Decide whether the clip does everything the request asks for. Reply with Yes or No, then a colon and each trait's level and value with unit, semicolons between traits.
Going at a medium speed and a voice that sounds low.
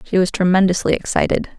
No: average, 150 wpm; medium, 185 Hz